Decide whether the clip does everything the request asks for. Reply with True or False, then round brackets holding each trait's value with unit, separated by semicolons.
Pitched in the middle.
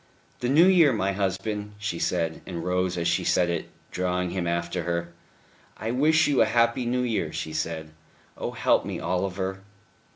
False (95 Hz)